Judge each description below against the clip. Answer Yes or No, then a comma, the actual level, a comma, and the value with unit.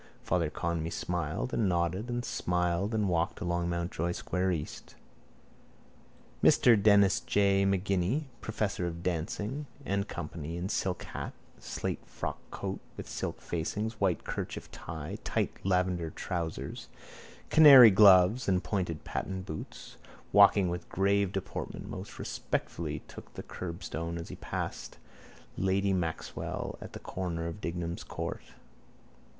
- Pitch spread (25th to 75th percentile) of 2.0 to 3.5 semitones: Yes, average, 2.8 semitones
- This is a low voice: Yes, very low, 90 Hz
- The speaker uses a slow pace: Yes, slow, 125 wpm